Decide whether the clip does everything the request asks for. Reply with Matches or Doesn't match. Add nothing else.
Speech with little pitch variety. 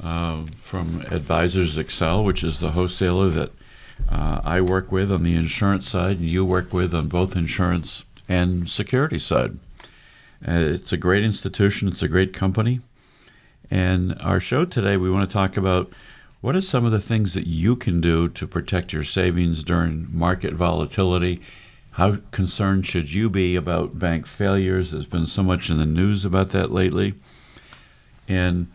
Matches